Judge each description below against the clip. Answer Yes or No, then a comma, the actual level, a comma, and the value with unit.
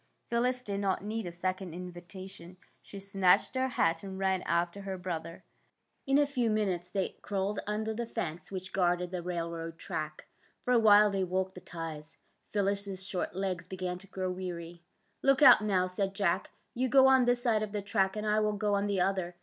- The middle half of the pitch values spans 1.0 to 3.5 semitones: Yes, average, 2.8 semitones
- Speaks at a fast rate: Yes, fast, 210 wpm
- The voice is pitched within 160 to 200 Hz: Yes, high, 190 Hz